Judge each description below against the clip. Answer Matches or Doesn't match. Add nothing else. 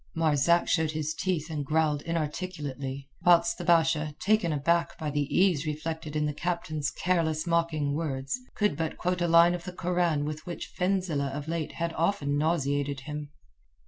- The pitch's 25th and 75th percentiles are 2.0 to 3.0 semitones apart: Matches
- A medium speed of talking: Matches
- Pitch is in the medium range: Matches